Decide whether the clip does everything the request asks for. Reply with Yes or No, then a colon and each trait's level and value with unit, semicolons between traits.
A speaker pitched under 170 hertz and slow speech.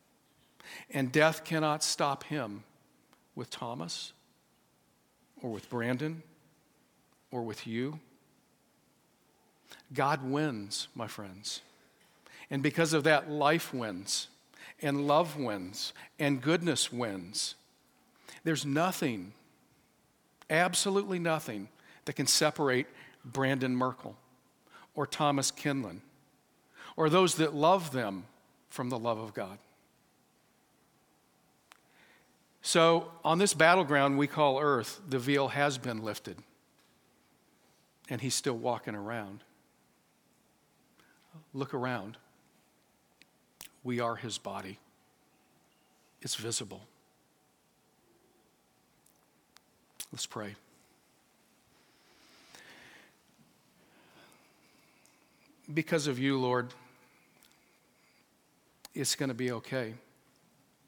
Yes: medium, 140 Hz; slow, 85 wpm